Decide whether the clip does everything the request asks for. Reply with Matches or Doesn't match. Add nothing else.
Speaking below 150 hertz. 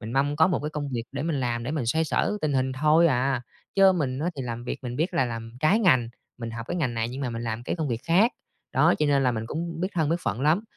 Matches